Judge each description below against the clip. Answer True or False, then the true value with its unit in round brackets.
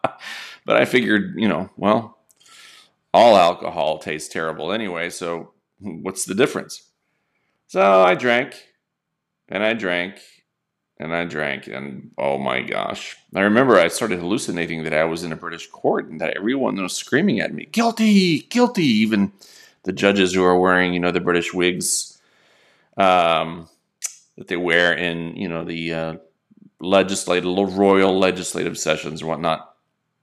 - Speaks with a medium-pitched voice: False (90 Hz)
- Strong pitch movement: False (2.8 semitones)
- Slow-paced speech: False (150 wpm)